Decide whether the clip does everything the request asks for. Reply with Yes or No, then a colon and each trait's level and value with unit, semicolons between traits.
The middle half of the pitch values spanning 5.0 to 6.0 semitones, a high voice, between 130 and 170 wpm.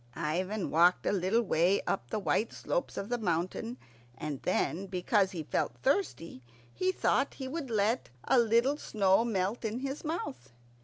Yes: wide, 5.4 semitones; high, 205 Hz; average, 165 wpm